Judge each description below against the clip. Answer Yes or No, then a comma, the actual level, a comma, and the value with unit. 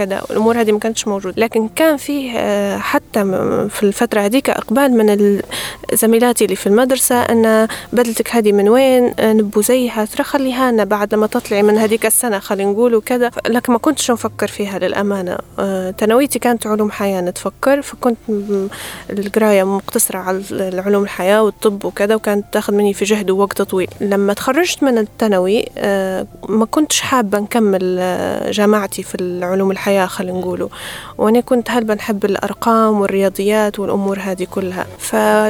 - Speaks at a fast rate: Yes, fast, 155 wpm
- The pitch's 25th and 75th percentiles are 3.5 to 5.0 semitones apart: No, average, 3.0 semitones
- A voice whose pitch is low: No, high, 215 Hz